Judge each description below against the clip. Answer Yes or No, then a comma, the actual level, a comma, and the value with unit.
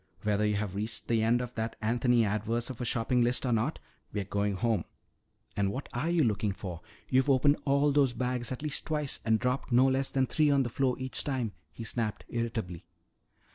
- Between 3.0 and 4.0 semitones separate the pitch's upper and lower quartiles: Yes, average, 3.5 semitones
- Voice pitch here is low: Yes, low, 120 Hz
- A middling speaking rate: No, fast, 210 wpm